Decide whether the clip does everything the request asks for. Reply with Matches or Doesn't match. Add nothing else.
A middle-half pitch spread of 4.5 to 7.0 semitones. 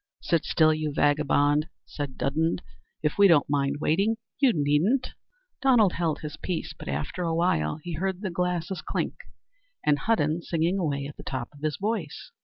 Doesn't match